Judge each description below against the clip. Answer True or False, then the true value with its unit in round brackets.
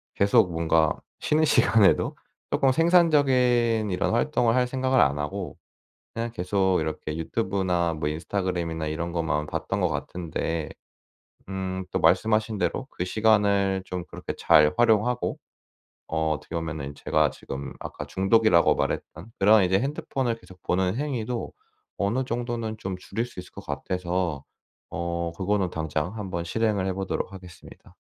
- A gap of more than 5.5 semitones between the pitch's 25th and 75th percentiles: False (5.1 semitones)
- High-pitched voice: False (95 Hz)